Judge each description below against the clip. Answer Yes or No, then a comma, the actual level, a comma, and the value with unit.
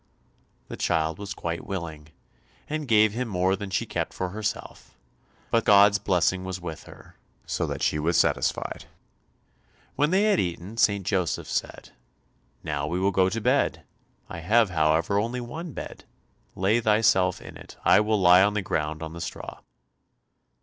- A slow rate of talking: No, average, 165 wpm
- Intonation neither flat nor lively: Yes, average, 4.2 semitones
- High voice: No, very low, 95 Hz